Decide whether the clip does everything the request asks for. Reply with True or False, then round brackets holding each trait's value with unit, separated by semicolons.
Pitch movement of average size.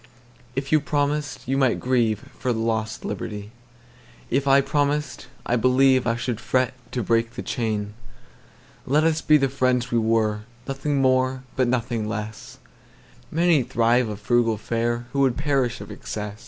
True (3.2 semitones)